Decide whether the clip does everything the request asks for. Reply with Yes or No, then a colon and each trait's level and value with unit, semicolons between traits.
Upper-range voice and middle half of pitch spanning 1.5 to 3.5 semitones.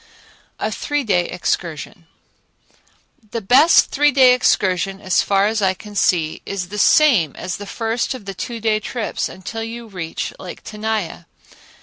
No: high, 210 Hz; average, 4.0 semitones